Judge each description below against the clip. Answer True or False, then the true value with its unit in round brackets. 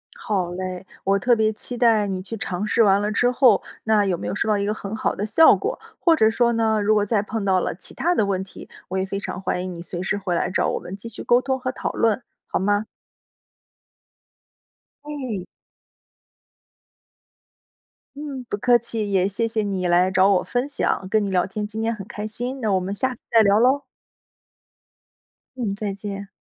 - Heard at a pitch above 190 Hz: True (210 Hz)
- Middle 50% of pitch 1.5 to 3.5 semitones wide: True (3.0 semitones)